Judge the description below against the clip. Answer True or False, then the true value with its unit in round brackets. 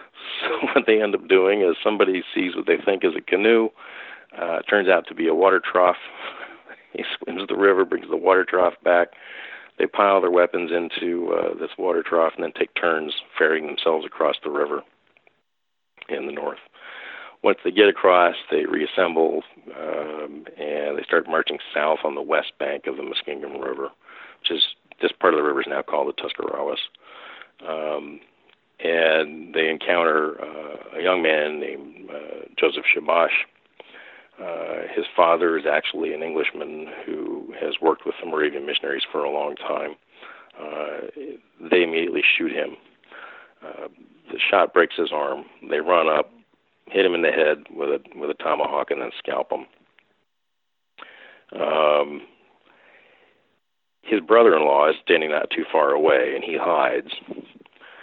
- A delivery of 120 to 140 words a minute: False (165 wpm)